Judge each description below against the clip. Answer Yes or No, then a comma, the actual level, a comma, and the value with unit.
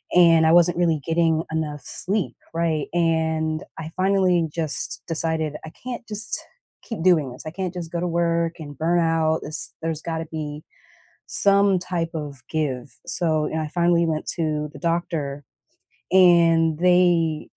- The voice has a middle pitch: Yes, medium, 165 Hz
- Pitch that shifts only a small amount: Yes, narrow, 1.8 semitones